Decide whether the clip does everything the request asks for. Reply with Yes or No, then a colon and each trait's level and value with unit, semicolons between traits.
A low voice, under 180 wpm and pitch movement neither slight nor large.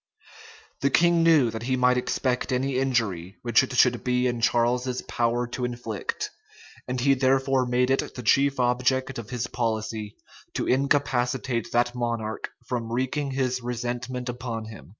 No: low, 125 Hz; average, 155 wpm; narrow, 1.7 semitones